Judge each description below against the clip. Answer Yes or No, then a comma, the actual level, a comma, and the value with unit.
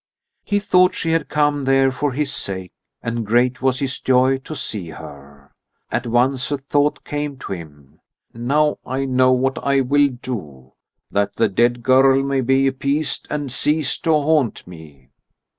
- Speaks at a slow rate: No, average, 165 wpm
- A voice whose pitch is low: Yes, low, 130 Hz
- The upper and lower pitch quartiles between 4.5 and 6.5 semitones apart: No, average, 3.6 semitones